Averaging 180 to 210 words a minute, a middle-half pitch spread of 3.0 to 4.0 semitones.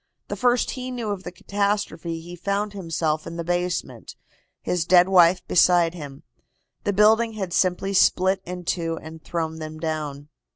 No: average, 165 wpm; average, 3.4 semitones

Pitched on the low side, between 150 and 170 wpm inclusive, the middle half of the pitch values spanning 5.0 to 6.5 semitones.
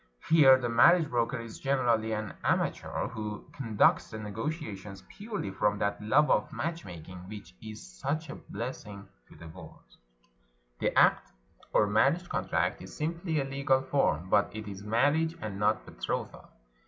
Yes: low, 110 Hz; average, 155 wpm; wide, 5.5 semitones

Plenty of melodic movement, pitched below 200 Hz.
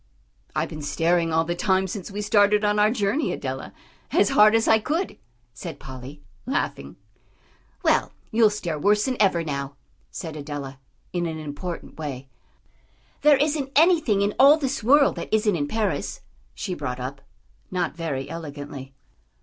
Yes: wide, 6.8 semitones; medium, 185 Hz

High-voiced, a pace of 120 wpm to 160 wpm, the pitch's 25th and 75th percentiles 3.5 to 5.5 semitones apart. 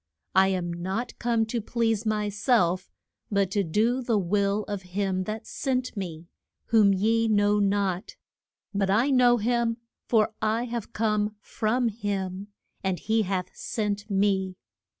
No: high, 210 Hz; average, 150 wpm; average, 2.8 semitones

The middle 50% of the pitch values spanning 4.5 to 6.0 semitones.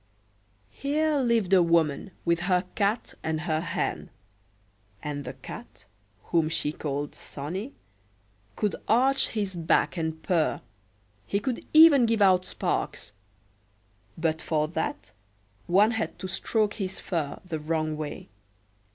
Yes: wide, 5.4 semitones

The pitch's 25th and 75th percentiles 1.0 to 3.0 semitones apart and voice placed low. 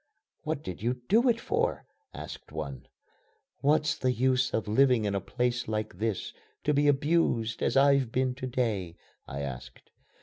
No: average, 4.5 semitones; low, 125 Hz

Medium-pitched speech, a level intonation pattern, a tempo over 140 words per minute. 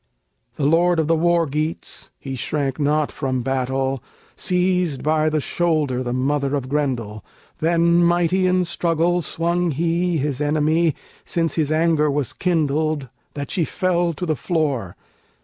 No: medium, 155 Hz; average, 3.5 semitones; average, 150 wpm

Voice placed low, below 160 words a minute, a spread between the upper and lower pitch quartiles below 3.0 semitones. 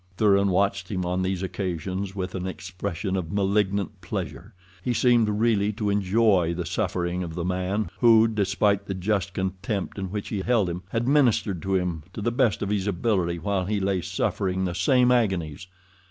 No: very low, 95 Hz; average, 180 wpm; narrow, 2.5 semitones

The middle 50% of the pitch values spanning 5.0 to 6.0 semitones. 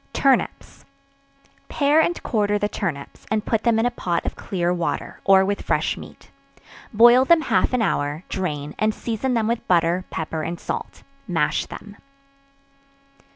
Yes: average, 5.3 semitones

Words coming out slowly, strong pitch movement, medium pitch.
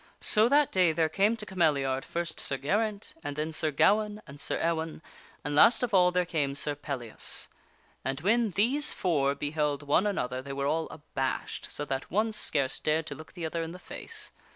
No: average, 200 wpm; wide, 5.7 semitones; medium, 160 Hz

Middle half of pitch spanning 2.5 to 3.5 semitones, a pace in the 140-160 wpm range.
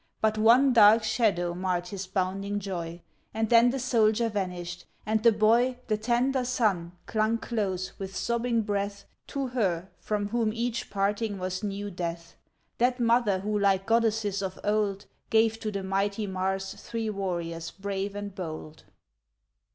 Yes: average, 3.0 semitones; average, 155 wpm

